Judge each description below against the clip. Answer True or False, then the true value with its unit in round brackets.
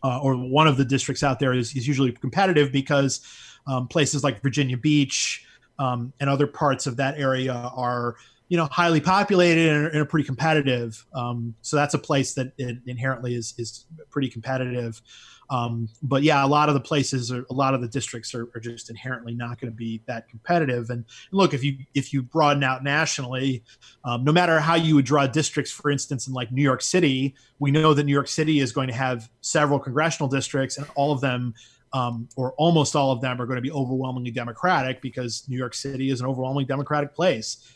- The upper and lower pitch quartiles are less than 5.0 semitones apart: True (2.8 semitones)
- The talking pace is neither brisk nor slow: False (215 wpm)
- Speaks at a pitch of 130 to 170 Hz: True (135 Hz)